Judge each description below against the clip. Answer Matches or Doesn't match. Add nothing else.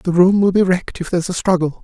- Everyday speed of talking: Doesn't match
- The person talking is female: Doesn't match